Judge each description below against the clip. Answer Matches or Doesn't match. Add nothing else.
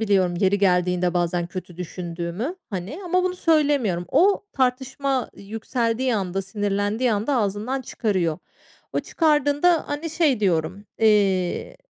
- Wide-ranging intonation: Matches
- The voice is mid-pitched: Doesn't match